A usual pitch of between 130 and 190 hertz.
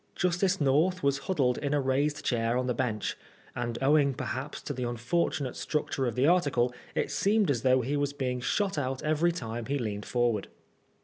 Yes: low, 135 Hz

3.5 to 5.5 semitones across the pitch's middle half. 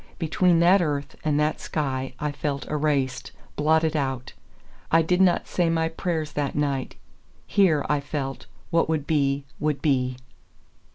No: narrow, 2.6 semitones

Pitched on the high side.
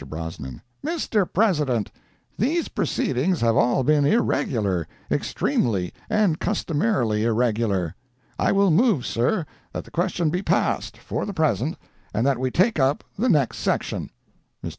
No: medium, 140 Hz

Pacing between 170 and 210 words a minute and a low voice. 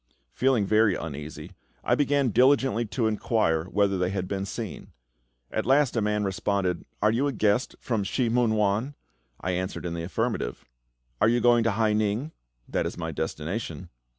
Yes: average, 175 wpm; low, 105 Hz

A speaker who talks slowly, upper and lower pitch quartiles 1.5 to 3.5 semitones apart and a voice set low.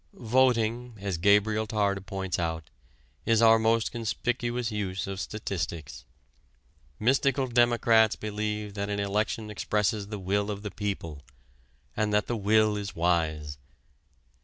Yes: slow, 130 wpm; narrow, 2.4 semitones; low, 105 Hz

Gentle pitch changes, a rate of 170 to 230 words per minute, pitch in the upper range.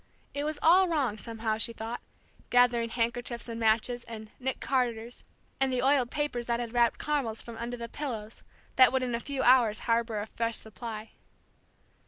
Yes: narrow, 2.2 semitones; average, 180 wpm; high, 235 Hz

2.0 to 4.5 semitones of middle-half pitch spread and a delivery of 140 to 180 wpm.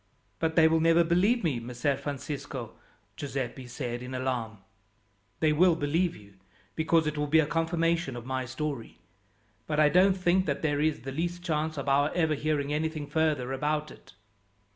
Yes: average, 3.5 semitones; average, 175 wpm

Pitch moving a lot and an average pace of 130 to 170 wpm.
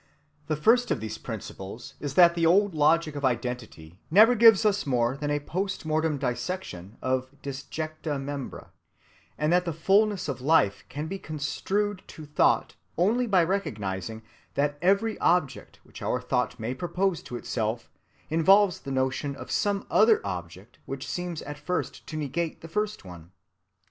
Yes: wide, 6.5 semitones; average, 160 wpm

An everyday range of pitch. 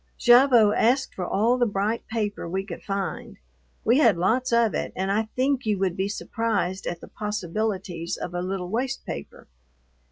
Yes: average, 3.7 semitones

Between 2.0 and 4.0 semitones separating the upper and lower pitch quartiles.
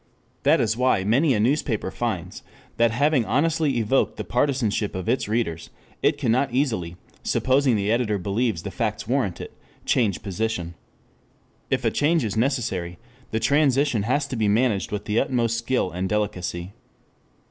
No: average, 4.4 semitones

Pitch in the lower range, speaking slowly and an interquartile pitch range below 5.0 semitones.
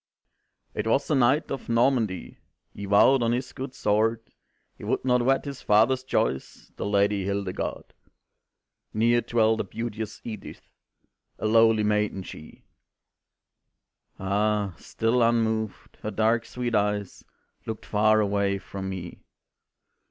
Yes: low, 110 Hz; slow, 130 wpm; narrow, 2.6 semitones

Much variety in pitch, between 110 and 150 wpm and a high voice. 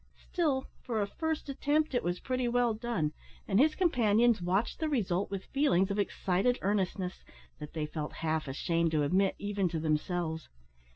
No: wide, 6.1 semitones; average, 170 wpm; high, 200 Hz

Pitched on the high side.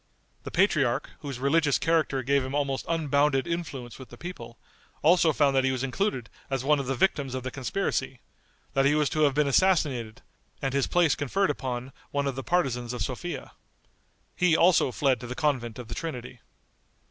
No: medium, 140 Hz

